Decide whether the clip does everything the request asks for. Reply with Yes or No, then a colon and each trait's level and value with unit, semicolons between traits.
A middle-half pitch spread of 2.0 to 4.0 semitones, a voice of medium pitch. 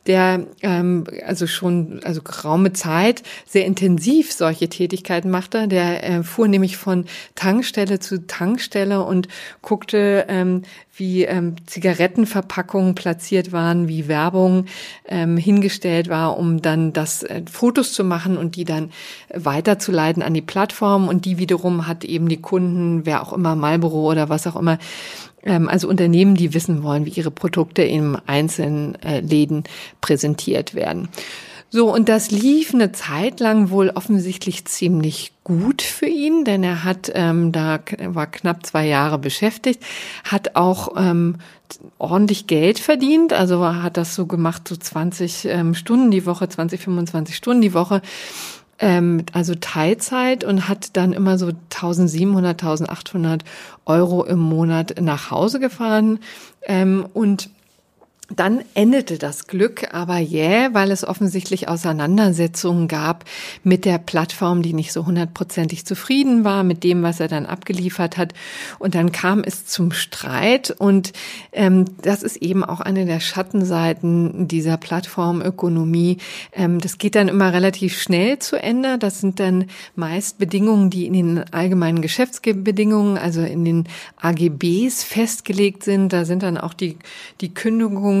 Yes: average, 2.8 semitones; medium, 180 Hz